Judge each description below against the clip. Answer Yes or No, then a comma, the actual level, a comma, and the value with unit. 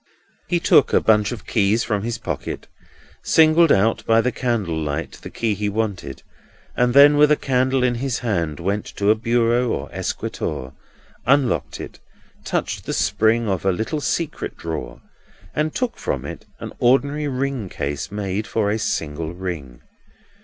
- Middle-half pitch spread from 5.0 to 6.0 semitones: Yes, wide, 5.6 semitones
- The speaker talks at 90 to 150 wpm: No, average, 165 wpm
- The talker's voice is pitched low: Yes, low, 110 Hz